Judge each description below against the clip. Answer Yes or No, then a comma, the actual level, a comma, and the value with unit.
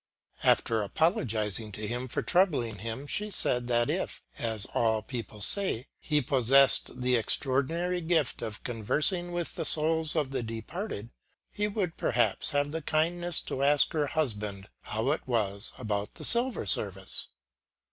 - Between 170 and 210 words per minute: No, average, 150 wpm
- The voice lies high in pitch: No, low, 130 Hz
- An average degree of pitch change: No, wide, 6.4 semitones